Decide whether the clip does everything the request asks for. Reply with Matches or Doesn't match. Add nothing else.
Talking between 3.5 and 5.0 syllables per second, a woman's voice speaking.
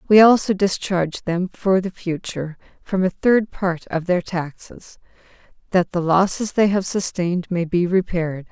Matches